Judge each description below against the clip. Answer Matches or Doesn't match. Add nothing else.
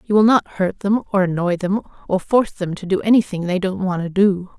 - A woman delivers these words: Matches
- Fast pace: Matches